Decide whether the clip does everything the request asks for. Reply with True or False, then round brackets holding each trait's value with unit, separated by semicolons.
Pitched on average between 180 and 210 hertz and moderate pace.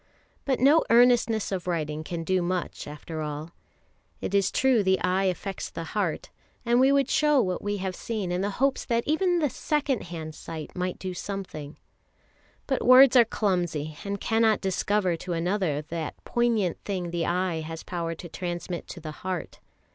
True (185 Hz; 180 wpm)